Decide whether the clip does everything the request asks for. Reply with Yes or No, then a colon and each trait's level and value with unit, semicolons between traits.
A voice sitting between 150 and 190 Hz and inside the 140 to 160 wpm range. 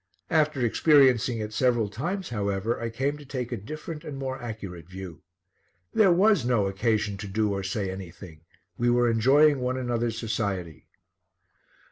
No: low, 115 Hz; average, 155 wpm